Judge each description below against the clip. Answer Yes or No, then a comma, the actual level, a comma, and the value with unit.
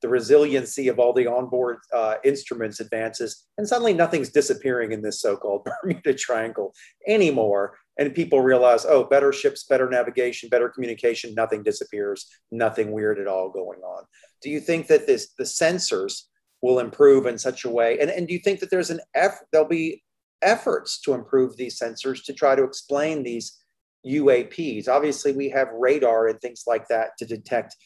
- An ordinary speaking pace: Yes, average, 175 wpm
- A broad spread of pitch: Yes, wide, 7.1 semitones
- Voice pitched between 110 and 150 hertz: Yes, low, 135 Hz